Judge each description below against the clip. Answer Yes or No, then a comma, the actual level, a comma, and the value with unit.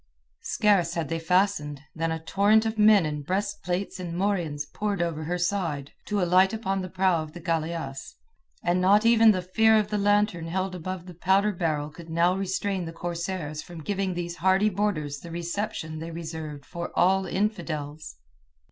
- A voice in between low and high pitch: Yes, medium, 180 Hz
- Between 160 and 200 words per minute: Yes, average, 180 wpm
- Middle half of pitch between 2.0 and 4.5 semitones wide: Yes, average, 3.4 semitones